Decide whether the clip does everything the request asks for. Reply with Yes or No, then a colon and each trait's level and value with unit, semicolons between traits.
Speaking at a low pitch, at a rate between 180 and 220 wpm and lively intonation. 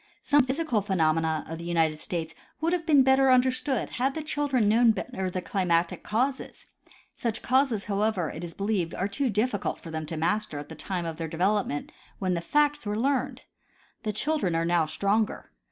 No: high, 205 Hz; average, 190 wpm; wide, 7.4 semitones